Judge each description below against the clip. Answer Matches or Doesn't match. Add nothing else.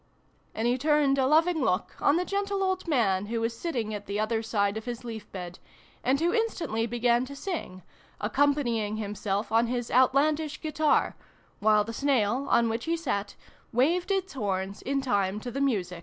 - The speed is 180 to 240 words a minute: Matches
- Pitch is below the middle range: Doesn't match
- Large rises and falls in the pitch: Matches